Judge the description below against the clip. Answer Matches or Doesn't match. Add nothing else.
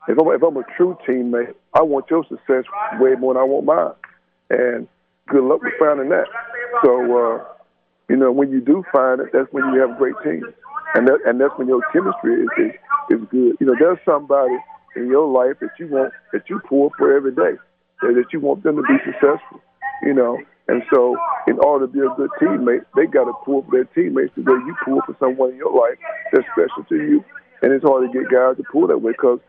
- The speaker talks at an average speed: Doesn't match